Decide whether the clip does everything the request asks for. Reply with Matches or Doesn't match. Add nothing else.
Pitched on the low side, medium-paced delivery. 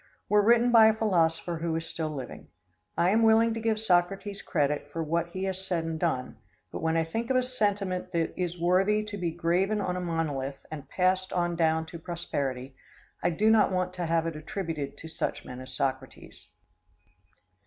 Doesn't match